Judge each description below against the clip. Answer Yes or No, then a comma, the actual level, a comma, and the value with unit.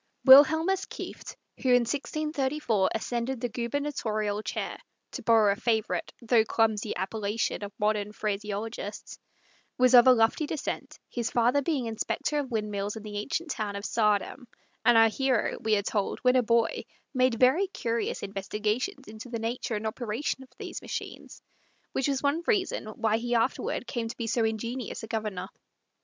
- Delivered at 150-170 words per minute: Yes, average, 165 wpm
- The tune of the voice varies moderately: Yes, average, 3.3 semitones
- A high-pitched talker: Yes, high, 230 Hz